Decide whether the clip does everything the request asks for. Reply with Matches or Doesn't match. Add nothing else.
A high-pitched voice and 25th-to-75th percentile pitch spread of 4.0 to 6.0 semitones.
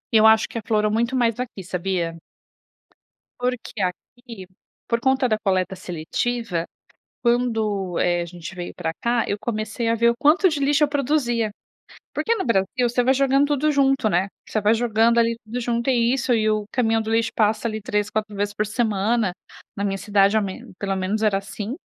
Doesn't match